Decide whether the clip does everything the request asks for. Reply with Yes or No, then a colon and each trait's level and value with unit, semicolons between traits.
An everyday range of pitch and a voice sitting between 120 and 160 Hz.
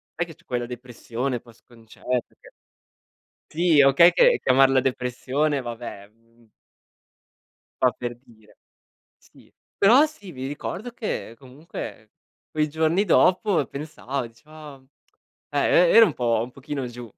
Yes: average, 4.6 semitones; low, 135 Hz